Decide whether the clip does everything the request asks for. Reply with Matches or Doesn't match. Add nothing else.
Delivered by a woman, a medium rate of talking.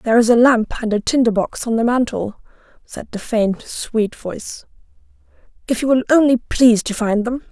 Matches